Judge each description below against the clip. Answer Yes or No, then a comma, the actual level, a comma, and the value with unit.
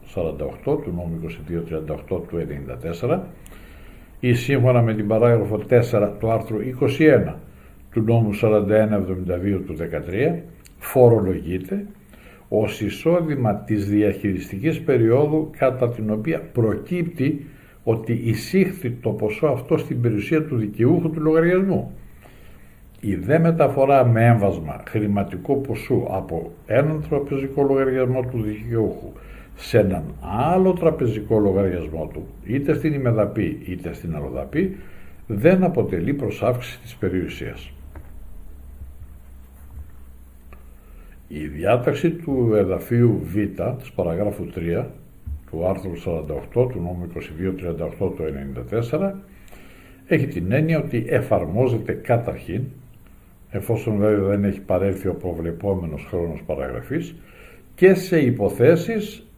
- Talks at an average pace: No, slow, 105 wpm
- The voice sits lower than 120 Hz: Yes, low, 105 Hz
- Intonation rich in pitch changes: Yes, wide, 6.9 semitones